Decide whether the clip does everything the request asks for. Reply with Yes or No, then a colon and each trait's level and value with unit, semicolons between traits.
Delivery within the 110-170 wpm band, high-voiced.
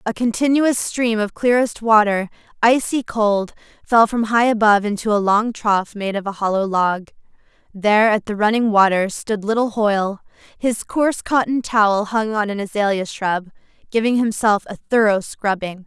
Yes: average, 165 wpm; high, 215 Hz